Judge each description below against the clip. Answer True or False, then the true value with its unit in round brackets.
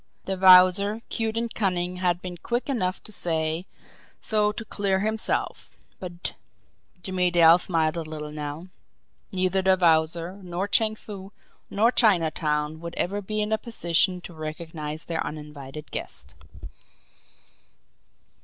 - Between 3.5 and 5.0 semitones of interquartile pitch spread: True (3.9 semitones)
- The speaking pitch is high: False (180 Hz)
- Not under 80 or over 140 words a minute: True (135 wpm)